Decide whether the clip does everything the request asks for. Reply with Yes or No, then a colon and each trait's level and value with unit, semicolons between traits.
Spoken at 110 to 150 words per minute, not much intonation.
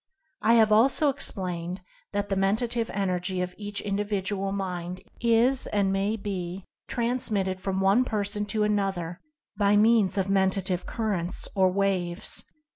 Yes: average, 140 wpm; narrow, 2.3 semitones